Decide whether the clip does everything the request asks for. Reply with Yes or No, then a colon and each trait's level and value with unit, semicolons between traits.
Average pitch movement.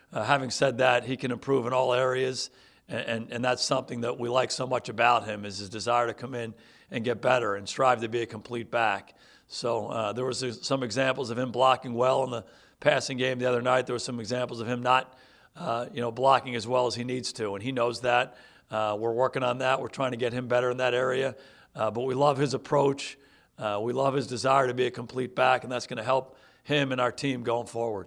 No: narrow, 1.5 semitones